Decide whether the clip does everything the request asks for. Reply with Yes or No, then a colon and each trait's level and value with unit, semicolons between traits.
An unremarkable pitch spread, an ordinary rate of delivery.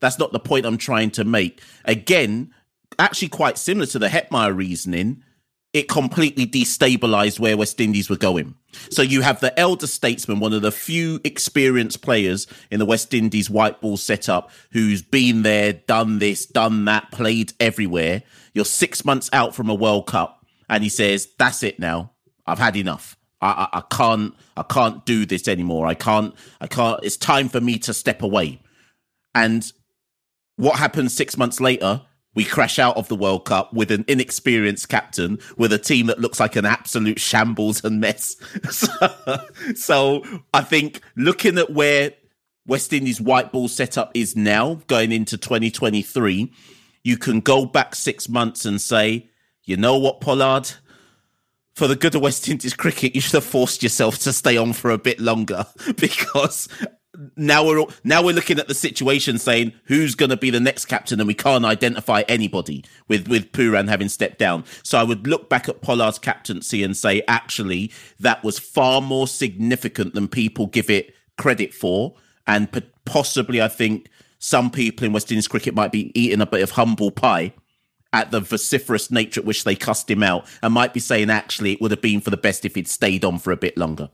Yes: average, 3.5 semitones; average, 190 wpm